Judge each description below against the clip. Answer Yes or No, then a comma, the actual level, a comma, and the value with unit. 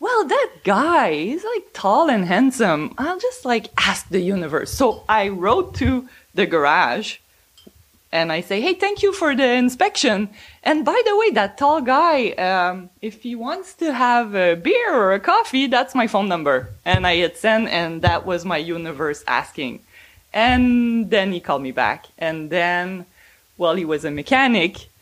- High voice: Yes, high, 220 Hz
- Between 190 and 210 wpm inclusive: No, average, 175 wpm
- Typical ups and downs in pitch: No, wide, 9.0 semitones